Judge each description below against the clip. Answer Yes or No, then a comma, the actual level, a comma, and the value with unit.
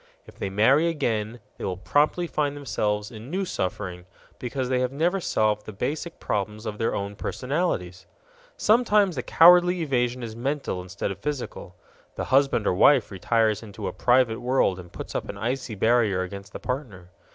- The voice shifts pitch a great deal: Yes, wide, 5.8 semitones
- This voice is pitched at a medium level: No, low, 120 Hz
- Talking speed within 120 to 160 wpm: No, average, 175 wpm